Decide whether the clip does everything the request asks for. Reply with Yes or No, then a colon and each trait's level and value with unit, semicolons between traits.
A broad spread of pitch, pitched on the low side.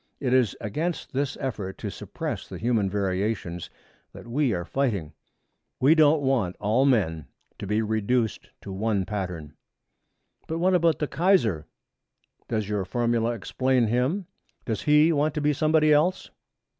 Yes: wide, 6.6 semitones; low, 120 Hz